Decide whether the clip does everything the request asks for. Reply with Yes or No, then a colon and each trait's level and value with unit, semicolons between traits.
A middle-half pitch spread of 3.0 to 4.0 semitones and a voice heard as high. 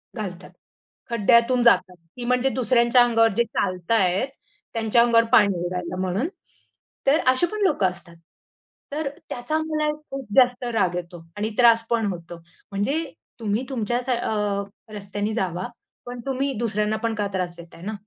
No: average, 4.4 semitones; high, 225 Hz